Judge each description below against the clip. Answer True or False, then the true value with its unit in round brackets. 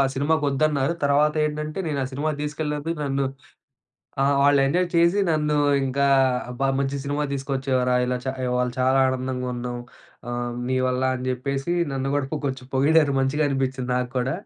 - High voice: False (135 Hz)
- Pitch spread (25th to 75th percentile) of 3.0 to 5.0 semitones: False (2.5 semitones)